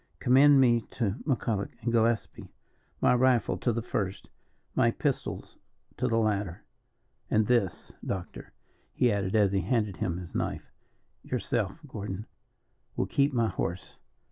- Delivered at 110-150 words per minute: Yes, average, 140 wpm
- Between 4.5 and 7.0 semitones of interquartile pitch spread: No, average, 3.8 semitones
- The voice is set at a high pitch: No, low, 110 Hz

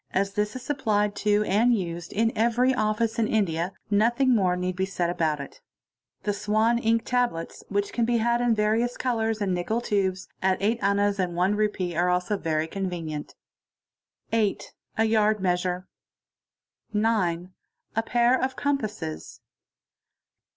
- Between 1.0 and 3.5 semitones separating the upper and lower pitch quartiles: No, average, 3.9 semitones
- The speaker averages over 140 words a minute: Yes, average, 150 wpm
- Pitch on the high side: Yes, high, 210 Hz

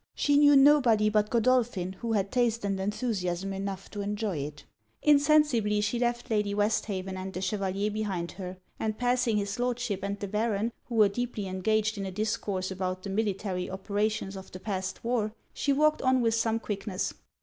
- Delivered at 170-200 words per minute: Yes, average, 180 wpm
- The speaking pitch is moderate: No, high, 210 Hz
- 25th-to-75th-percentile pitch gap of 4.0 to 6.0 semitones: No, average, 3.3 semitones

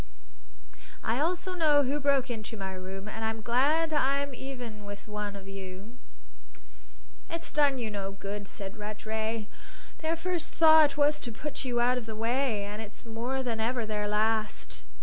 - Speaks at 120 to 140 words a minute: No, average, 170 wpm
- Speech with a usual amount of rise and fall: Yes, average, 5.0 semitones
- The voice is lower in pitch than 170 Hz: No, high, 230 Hz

